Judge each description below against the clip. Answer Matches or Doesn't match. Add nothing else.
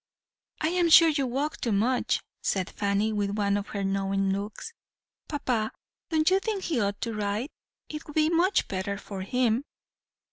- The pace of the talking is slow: Doesn't match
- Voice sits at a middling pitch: Doesn't match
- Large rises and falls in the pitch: Matches